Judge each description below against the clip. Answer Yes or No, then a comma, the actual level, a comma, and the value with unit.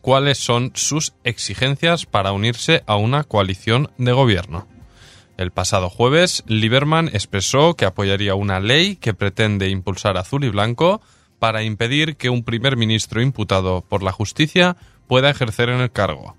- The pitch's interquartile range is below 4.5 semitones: No, average, 5.3 semitones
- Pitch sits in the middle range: No, low, 115 Hz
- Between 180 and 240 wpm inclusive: No, average, 150 wpm